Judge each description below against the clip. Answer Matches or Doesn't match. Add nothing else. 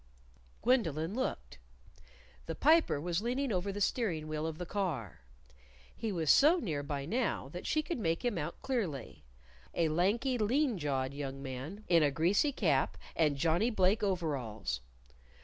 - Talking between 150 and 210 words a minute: Matches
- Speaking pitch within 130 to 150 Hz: Doesn't match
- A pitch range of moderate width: Doesn't match